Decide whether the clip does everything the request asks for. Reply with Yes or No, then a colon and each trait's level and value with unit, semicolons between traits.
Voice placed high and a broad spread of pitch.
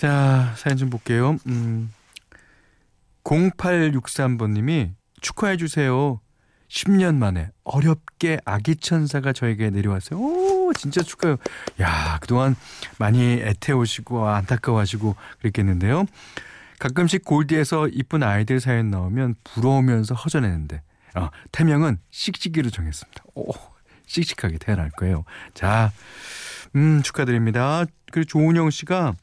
No: low, 130 Hz; wide, 6.9 semitones